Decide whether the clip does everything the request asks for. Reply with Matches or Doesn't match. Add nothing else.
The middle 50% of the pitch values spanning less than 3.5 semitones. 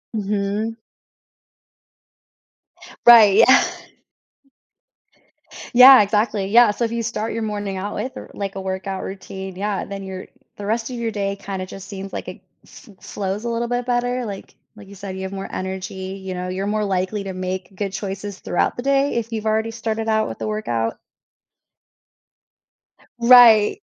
Matches